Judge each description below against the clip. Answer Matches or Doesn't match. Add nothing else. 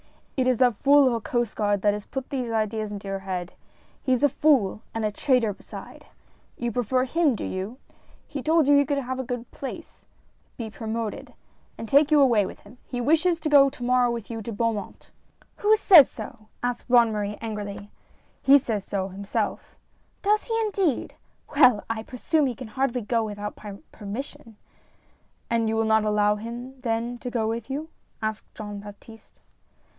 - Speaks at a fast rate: Matches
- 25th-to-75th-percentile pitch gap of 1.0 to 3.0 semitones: Doesn't match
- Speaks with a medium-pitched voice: Doesn't match